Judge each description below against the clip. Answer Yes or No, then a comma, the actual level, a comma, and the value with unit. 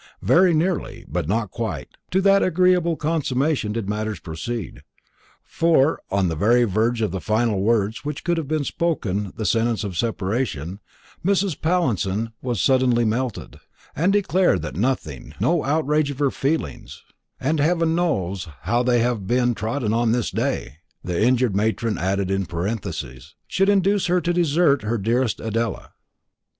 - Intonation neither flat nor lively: No, wide, 7.4 semitones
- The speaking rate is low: No, average, 155 wpm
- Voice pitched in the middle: No, low, 120 Hz